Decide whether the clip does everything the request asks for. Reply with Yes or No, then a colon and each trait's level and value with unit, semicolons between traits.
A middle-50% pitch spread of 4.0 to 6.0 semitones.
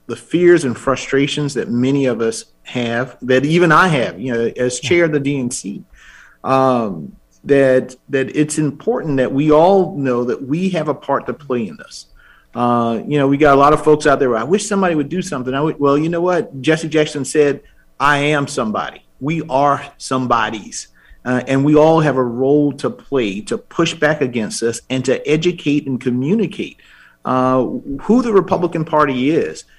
No: average, 3.4 semitones